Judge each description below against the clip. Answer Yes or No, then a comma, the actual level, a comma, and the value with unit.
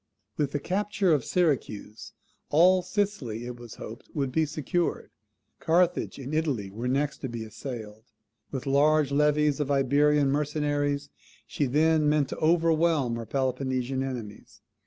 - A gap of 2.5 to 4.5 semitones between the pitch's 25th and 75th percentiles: Yes, average, 3.4 semitones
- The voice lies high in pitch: No, medium, 145 Hz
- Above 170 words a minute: No, average, 140 wpm